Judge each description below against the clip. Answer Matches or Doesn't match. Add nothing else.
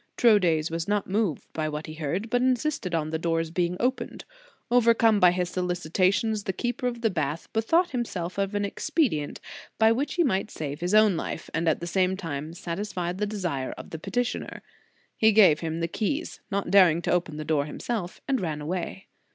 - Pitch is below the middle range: Doesn't match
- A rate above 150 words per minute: Matches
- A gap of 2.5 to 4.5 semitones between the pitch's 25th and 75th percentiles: Doesn't match